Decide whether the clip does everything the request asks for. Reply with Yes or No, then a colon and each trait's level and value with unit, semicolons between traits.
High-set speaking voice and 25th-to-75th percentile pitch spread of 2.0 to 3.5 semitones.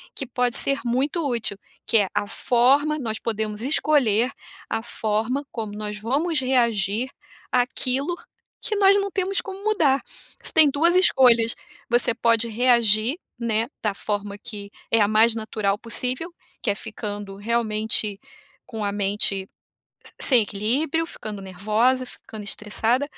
No: high, 230 Hz; average, 4.0 semitones